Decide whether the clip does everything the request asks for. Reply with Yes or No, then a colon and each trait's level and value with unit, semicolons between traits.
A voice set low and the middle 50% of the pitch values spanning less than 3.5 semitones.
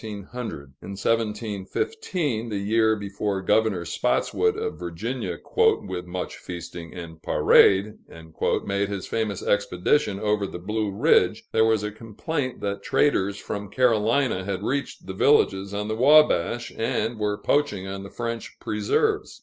Yes: low, 105 Hz; average, 3.1 semitones